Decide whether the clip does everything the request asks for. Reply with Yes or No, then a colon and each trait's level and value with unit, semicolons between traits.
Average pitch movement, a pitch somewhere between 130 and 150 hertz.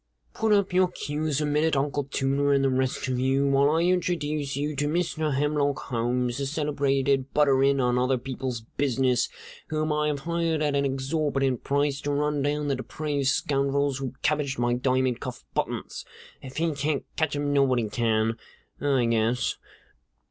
No: narrow, 2.2 semitones; medium, 140 Hz